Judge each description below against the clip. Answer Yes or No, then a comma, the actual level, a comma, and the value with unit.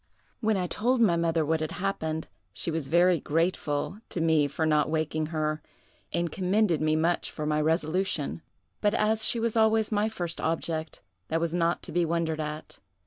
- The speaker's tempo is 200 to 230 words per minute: No, average, 185 wpm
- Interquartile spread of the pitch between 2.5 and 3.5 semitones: Yes, average, 3.2 semitones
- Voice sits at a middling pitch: Yes, medium, 165 Hz